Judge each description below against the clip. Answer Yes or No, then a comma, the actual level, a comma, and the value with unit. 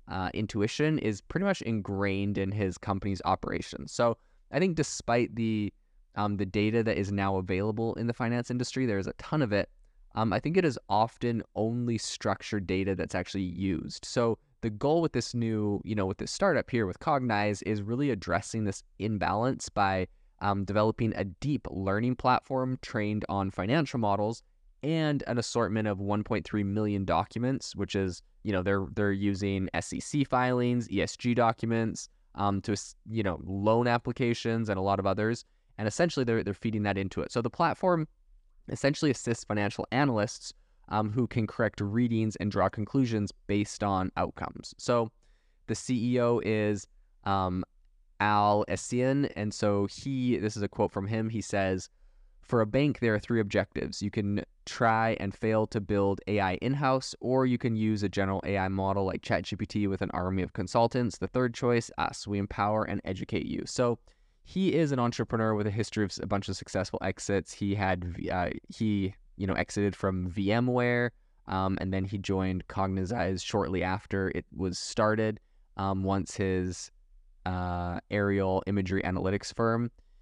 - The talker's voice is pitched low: Yes, low, 105 Hz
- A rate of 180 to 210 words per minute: No, average, 170 wpm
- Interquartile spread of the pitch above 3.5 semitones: No, average, 3.2 semitones